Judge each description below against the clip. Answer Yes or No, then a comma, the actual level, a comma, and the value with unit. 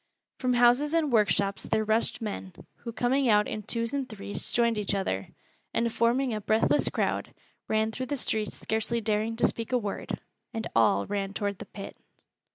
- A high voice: Yes, high, 220 Hz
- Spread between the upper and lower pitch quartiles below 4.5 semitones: Yes, average, 2.7 semitones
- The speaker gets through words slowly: No, average, 180 wpm